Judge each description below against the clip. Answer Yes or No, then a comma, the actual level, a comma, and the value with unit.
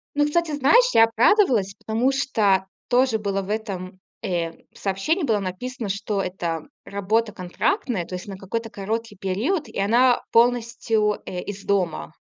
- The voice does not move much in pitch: No, average, 4.3 semitones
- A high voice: Yes, high, 215 Hz